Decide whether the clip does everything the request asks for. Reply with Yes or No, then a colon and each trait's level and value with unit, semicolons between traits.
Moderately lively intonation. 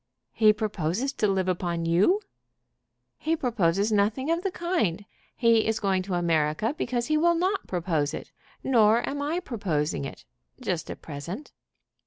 No: wide, 7.9 semitones